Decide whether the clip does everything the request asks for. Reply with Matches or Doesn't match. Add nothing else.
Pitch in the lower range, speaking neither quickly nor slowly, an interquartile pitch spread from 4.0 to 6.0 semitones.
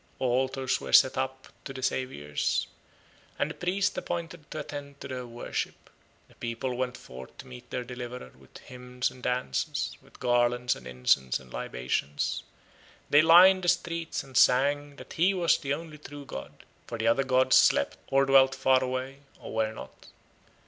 Doesn't match